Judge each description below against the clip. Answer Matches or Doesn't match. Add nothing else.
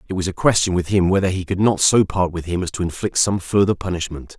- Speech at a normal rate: Doesn't match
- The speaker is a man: Matches